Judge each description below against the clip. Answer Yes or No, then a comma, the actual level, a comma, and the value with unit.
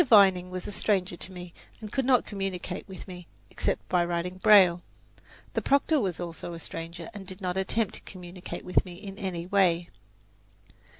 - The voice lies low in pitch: No, medium, 185 Hz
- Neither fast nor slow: Yes, average, 180 wpm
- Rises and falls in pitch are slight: Yes, narrow, 2.1 semitones